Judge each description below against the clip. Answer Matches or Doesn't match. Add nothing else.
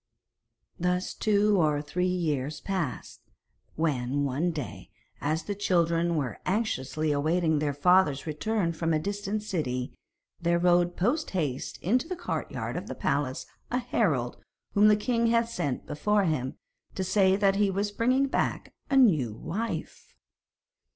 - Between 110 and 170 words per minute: Matches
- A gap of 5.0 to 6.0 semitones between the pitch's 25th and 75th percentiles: Matches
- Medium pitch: Matches